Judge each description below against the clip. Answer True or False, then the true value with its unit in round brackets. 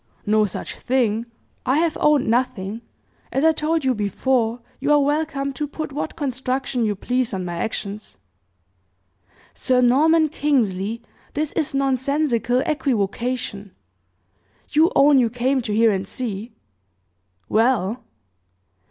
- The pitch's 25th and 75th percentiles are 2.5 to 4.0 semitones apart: False (4.5 semitones)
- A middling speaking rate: False (125 wpm)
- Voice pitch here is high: True (255 Hz)